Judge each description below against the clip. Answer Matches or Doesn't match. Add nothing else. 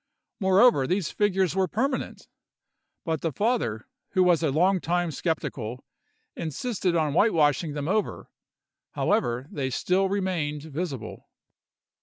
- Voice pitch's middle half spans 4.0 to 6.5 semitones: Matches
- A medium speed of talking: Doesn't match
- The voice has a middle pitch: Matches